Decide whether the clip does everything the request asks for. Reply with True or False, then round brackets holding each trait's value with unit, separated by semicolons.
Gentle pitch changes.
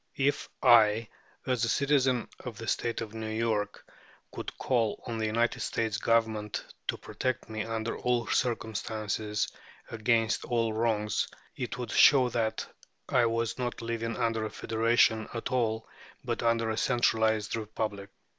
True (1.4 semitones)